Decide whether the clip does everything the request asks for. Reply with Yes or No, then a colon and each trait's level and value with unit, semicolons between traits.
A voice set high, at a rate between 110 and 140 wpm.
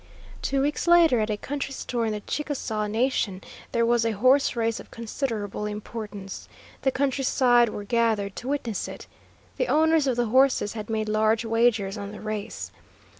No: high, 230 Hz; average, 175 wpm